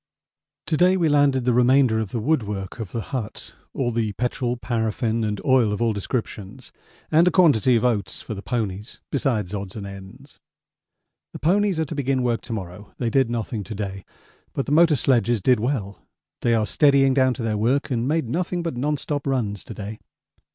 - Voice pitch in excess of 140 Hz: No, low, 120 Hz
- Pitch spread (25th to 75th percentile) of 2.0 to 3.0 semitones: No, average, 4.3 semitones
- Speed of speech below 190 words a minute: No, average, 200 wpm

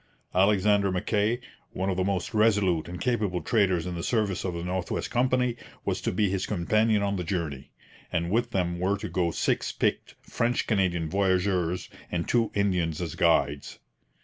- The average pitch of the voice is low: Yes, very low, 95 Hz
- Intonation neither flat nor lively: Yes, average, 3.2 semitones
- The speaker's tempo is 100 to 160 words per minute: No, average, 175 wpm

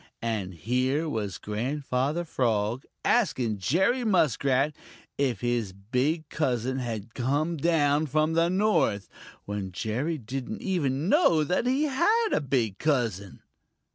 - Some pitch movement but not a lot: No, wide, 6.3 semitones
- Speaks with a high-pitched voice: No, low, 135 Hz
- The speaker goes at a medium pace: No, slow, 125 wpm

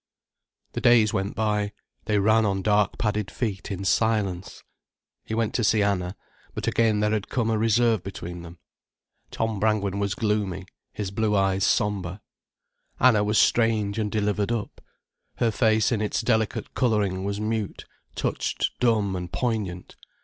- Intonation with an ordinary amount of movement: No, narrow, 2.1 semitones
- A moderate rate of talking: Yes, average, 155 wpm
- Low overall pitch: Yes, low, 105 Hz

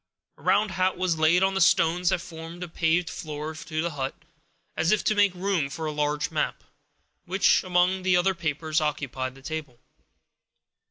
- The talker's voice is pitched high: No, medium, 165 Hz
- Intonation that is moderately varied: Yes, average, 3.1 semitones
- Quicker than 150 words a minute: Yes, average, 180 wpm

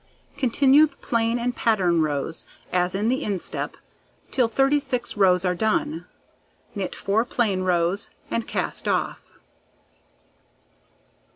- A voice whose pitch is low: No, high, 220 Hz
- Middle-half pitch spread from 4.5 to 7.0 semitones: Yes, average, 5.3 semitones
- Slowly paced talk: Yes, slow, 115 wpm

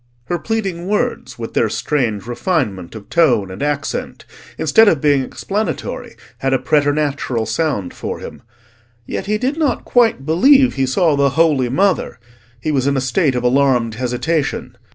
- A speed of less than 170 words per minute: Yes, average, 160 wpm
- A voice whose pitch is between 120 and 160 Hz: Yes, medium, 140 Hz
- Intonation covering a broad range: Yes, wide, 6.1 semitones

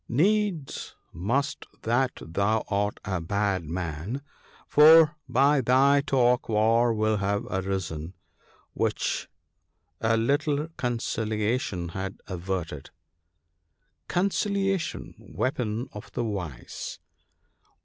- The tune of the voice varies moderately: No, wide, 6.3 semitones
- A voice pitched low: Yes, low, 110 Hz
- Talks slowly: Yes, slow, 100 wpm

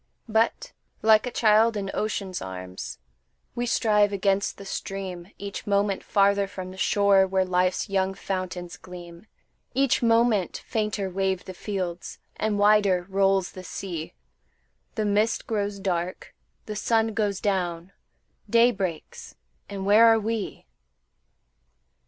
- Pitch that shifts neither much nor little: No, narrow, 2.3 semitones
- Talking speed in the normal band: No, slow, 130 wpm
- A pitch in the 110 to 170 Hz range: No, high, 200 Hz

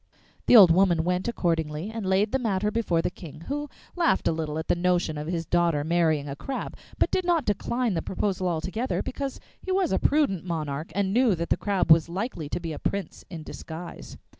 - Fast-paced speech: Yes, fast, 215 wpm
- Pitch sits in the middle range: Yes, medium, 180 Hz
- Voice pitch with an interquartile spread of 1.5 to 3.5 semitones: No, average, 5.2 semitones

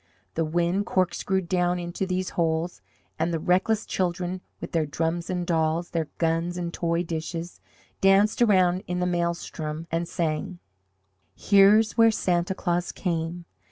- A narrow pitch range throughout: Yes, narrow, 1.8 semitones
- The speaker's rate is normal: Yes, average, 145 wpm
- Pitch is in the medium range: Yes, medium, 175 Hz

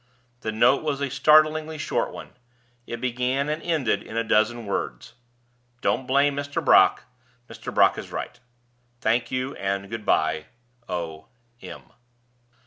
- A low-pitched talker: Yes, low, 125 Hz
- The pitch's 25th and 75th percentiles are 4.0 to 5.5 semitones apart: Yes, average, 4.7 semitones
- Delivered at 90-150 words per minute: Yes, average, 140 wpm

